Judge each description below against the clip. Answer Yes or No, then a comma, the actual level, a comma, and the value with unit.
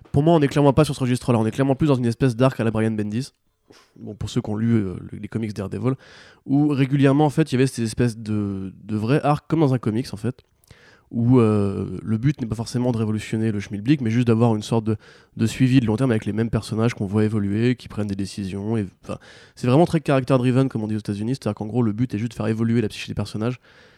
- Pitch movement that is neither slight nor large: Yes, average, 3.5 semitones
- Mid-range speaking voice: No, low, 115 Hz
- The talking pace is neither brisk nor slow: No, fast, 280 wpm